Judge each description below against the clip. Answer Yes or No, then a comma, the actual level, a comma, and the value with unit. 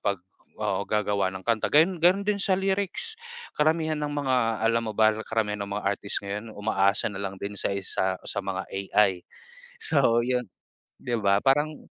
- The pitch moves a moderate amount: No, wide, 6.9 semitones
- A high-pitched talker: No, low, 110 Hz